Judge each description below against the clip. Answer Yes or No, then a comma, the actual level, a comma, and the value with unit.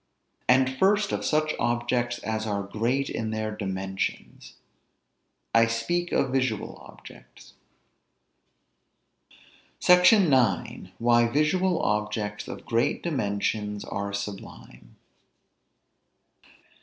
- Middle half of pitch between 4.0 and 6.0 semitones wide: Yes, average, 4.6 semitones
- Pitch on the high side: No, low, 115 Hz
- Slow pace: Yes, slow, 95 wpm